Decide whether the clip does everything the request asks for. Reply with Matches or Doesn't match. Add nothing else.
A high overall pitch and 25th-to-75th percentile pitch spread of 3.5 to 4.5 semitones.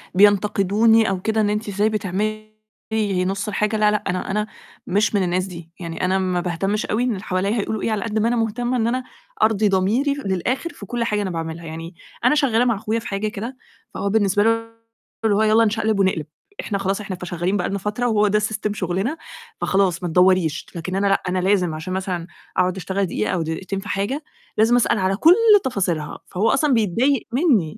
Doesn't match